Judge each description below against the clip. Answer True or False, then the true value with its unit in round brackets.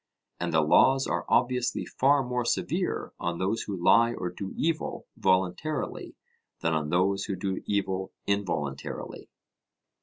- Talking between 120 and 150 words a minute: True (140 wpm)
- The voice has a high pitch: False (100 Hz)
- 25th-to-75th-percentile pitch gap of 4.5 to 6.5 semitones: True (5.5 semitones)